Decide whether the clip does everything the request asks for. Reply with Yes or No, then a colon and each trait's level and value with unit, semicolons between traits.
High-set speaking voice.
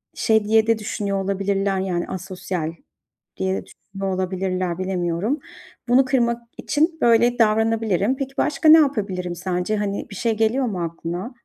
Yes: high, 200 Hz